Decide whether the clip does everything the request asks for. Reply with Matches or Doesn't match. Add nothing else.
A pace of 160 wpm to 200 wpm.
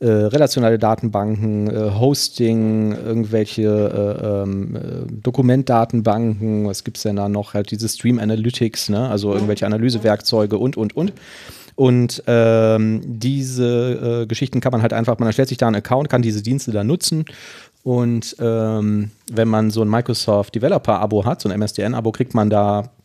Matches